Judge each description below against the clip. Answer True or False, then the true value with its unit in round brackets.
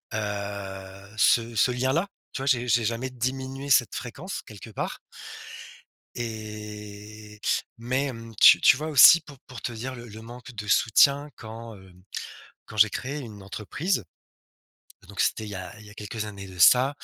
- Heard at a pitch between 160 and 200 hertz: False (115 Hz)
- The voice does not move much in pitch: False (3.7 semitones)